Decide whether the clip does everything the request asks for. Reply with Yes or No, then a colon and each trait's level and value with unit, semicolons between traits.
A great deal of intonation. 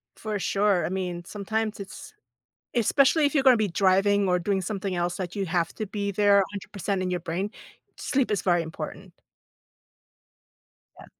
No: narrow, 2.6 semitones